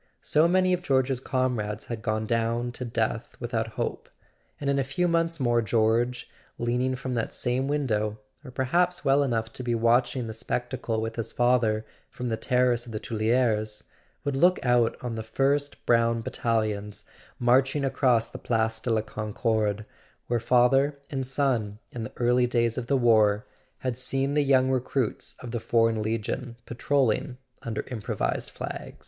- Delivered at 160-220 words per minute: Yes, average, 165 wpm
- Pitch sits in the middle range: No, low, 120 Hz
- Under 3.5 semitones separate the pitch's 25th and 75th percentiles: Yes, average, 2.8 semitones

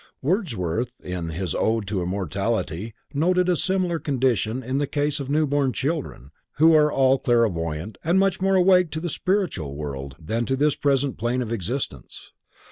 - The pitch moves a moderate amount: No, wide, 8.3 semitones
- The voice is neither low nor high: No, low, 130 Hz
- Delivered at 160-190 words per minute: Yes, average, 170 wpm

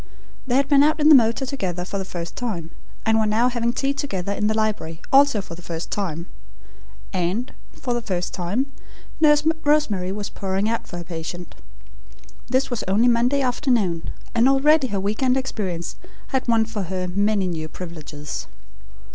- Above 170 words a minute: Yes, average, 180 wpm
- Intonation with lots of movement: Yes, wide, 6.0 semitones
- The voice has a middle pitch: No, high, 215 Hz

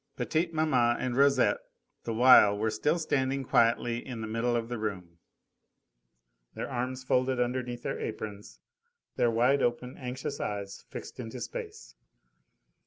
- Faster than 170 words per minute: No, average, 140 wpm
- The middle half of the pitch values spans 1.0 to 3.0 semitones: Yes, narrow, 2.5 semitones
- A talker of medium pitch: No, low, 125 Hz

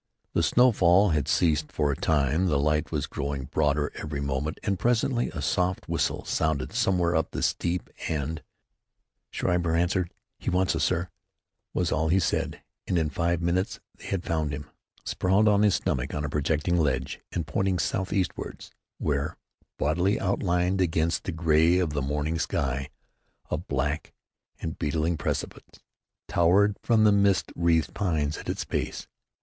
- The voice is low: Yes, very low, 80 Hz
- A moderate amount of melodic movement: Yes, average, 3.6 semitones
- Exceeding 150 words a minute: Yes, average, 160 wpm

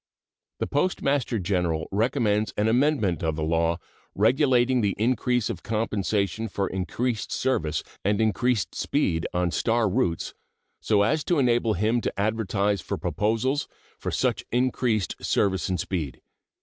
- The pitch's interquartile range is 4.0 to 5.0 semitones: Yes, average, 4.5 semitones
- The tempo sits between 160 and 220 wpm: No, slow, 135 wpm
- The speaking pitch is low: Yes, low, 110 Hz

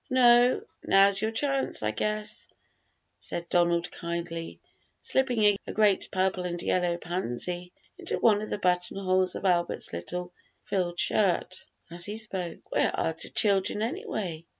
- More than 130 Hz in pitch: Yes, medium, 185 Hz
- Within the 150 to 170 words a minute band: No, average, 140 wpm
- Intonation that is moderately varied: Yes, average, 3.5 semitones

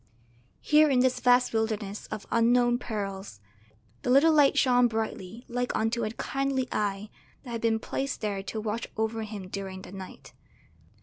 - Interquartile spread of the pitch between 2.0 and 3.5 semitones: Yes, average, 3.1 semitones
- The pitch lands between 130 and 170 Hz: No, high, 225 Hz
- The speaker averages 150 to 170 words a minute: Yes, average, 165 wpm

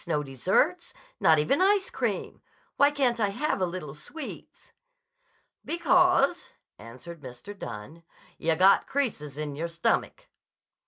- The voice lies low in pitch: No, medium, 185 Hz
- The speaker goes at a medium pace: No, slow, 125 wpm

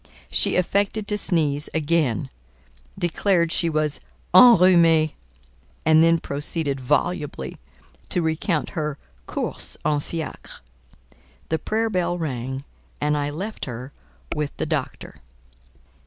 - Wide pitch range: No, average, 3.2 semitones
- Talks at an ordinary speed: No, slow, 110 wpm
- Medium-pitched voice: Yes, medium, 160 Hz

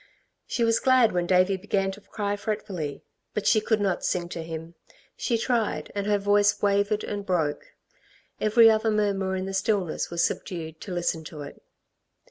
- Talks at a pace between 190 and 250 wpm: No, average, 175 wpm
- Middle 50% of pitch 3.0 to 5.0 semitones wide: Yes, average, 3.3 semitones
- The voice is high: Yes, high, 200 Hz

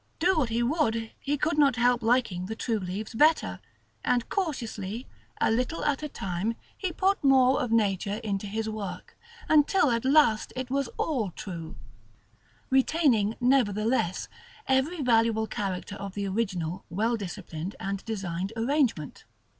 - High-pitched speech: Yes, high, 230 Hz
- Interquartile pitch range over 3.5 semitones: Yes, average, 5.1 semitones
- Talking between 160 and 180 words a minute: No, average, 145 wpm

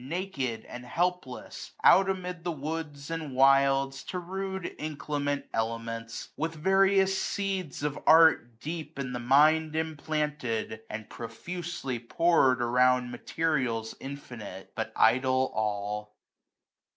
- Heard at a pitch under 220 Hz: Yes, medium, 140 Hz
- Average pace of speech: No, slow, 115 wpm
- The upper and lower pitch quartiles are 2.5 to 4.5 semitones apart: No, average, 5.1 semitones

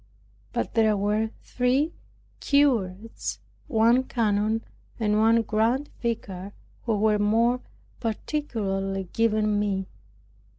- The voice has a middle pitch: No, high, 220 Hz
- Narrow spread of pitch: Yes, narrow, 2.2 semitones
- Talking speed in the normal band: No, slow, 95 wpm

